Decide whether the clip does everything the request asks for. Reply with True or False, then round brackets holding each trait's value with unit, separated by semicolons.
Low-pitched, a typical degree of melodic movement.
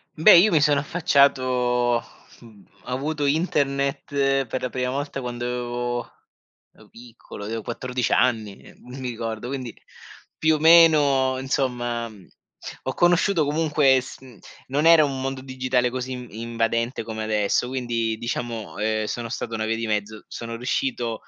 True (125 Hz; 3.0 semitones)